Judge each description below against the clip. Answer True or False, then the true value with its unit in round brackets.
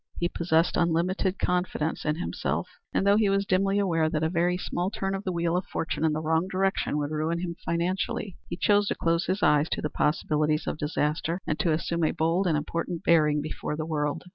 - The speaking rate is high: True (220 wpm)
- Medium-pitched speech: True (170 Hz)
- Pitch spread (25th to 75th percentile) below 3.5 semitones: True (2.9 semitones)